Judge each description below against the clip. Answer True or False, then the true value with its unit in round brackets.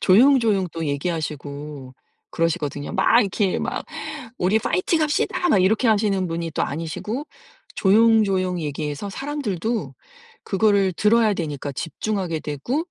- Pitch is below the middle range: False (190 Hz)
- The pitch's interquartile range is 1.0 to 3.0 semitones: False (5.6 semitones)